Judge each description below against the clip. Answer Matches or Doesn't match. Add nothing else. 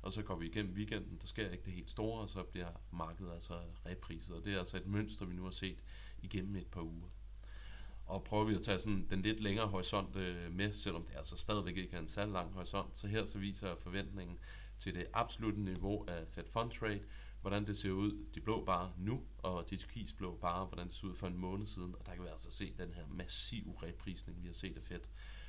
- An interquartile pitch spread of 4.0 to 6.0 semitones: Doesn't match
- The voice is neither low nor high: Doesn't match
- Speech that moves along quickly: Matches